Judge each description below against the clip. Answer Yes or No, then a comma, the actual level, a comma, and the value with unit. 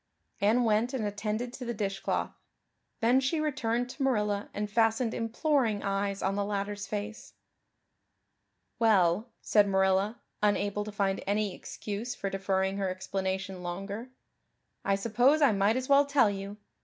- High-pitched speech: Yes, high, 210 Hz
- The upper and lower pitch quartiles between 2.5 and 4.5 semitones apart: Yes, average, 3.1 semitones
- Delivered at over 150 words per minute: No, average, 145 wpm